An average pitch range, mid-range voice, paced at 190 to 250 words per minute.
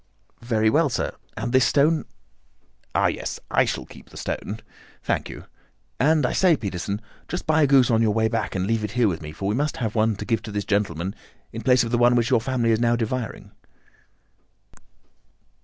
No: average, 3.2 semitones; low, 115 Hz; fast, 205 wpm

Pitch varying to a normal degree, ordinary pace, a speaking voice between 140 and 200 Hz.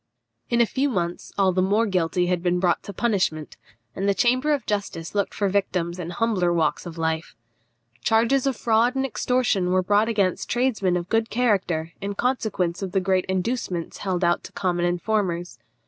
Yes: average, 4.2 semitones; average, 185 wpm; high, 190 Hz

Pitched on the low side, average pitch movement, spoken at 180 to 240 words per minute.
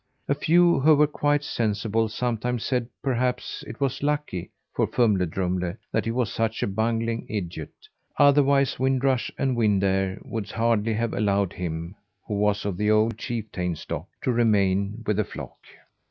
No: low, 115 Hz; average, 4.3 semitones; average, 170 wpm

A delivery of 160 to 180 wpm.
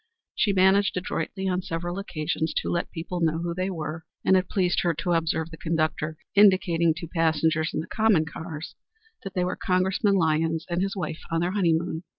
No: average, 190 wpm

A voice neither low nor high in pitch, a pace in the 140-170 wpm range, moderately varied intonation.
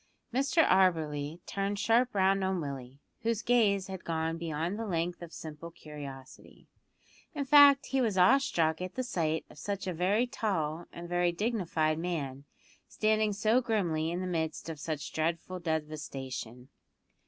Yes: medium, 175 Hz; average, 155 wpm; average, 4.9 semitones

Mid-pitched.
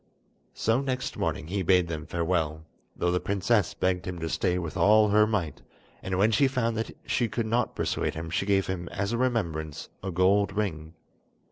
No: very low, 95 Hz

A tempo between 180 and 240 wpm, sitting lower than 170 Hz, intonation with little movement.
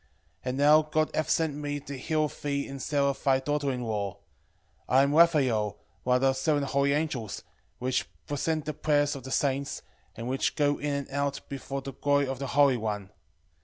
Yes: average, 200 wpm; medium, 140 Hz; narrow, 1.8 semitones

